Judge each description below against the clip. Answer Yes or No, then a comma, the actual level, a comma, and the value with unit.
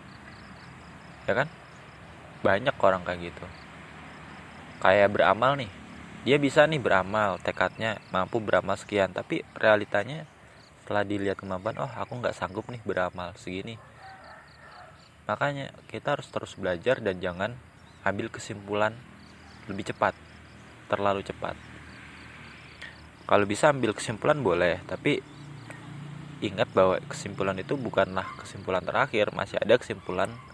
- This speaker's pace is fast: No, average, 110 wpm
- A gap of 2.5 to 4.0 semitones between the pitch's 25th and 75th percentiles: No, average, 4.9 semitones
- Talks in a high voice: No, low, 105 Hz